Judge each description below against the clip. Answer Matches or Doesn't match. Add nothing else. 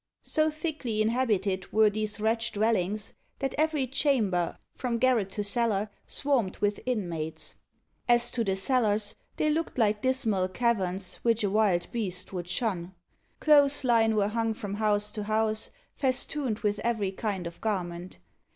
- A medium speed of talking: Matches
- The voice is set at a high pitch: Matches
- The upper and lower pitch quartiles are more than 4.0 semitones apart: Doesn't match